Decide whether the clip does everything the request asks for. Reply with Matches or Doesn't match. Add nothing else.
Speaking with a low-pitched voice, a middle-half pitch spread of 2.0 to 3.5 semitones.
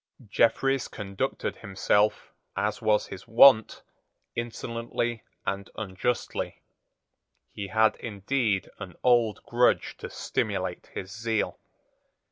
Matches